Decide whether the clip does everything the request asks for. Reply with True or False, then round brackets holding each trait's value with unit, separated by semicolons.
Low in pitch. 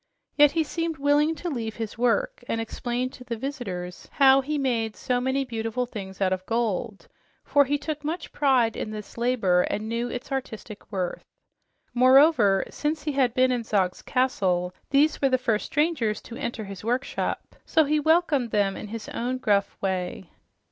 False (245 Hz)